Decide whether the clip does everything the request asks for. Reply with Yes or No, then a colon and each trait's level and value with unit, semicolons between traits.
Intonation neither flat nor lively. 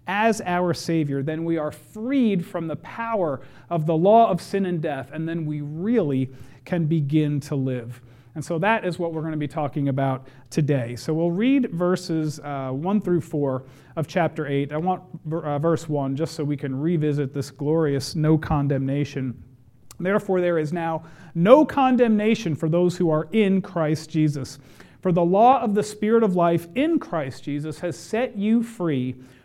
Yes: average, 4.0 semitones